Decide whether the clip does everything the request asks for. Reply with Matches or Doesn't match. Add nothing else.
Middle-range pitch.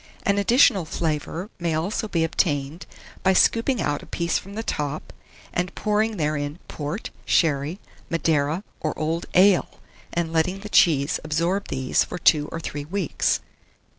Matches